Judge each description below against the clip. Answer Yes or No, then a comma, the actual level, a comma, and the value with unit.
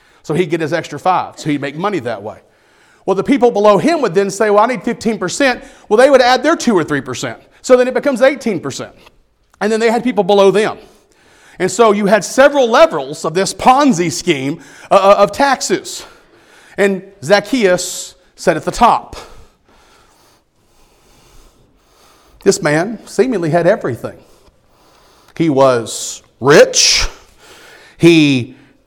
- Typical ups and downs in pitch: No, wide, 6.5 semitones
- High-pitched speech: Yes, high, 205 Hz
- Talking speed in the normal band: Yes, average, 150 wpm